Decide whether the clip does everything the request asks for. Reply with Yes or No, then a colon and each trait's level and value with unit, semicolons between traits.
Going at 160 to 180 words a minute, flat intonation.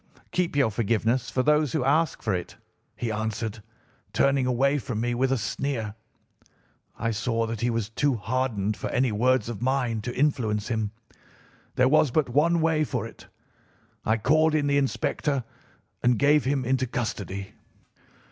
No: average, 165 wpm; average, 4.0 semitones